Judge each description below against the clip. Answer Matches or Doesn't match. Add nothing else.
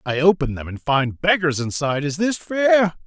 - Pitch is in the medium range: Matches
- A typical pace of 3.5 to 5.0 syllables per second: Matches